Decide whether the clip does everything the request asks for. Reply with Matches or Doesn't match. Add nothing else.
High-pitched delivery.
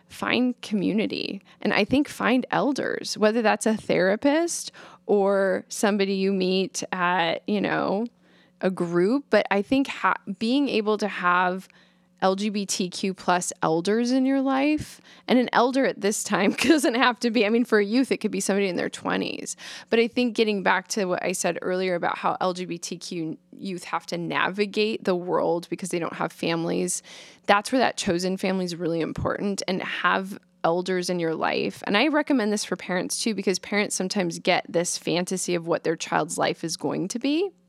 Matches